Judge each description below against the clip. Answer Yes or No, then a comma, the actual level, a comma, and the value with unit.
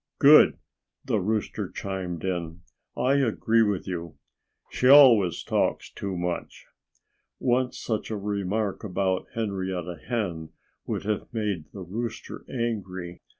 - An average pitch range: Yes, average, 4.1 semitones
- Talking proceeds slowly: Yes, slow, 120 wpm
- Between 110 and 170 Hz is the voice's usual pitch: No, low, 100 Hz